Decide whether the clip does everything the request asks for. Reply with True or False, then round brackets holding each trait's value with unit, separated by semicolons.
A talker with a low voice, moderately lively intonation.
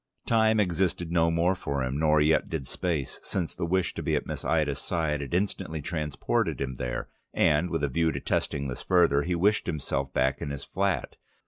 True (80 Hz; 3.9 semitones)